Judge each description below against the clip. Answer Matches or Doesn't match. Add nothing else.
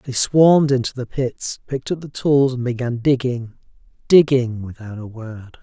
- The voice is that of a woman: Doesn't match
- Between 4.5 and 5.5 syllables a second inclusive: Matches